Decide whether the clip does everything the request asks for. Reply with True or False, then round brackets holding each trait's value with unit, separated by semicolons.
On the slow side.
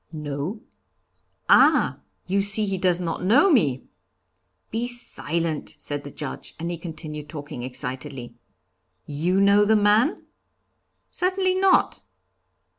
True (115 wpm)